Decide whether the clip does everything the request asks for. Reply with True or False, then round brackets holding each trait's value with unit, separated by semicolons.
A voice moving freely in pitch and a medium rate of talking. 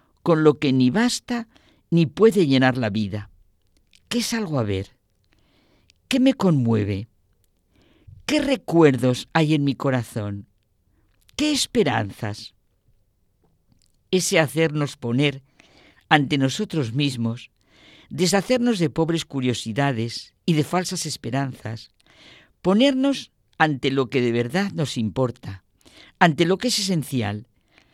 False (7.9 semitones; 115 wpm)